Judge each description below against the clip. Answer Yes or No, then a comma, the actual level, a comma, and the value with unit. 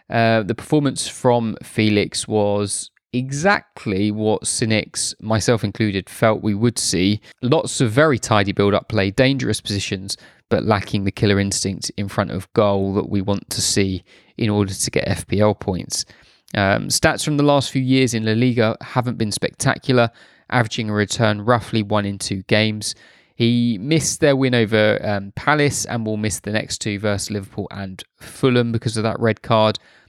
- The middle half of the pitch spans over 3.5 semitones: No, average, 3.0 semitones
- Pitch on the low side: Yes, low, 110 Hz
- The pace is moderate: Yes, average, 175 wpm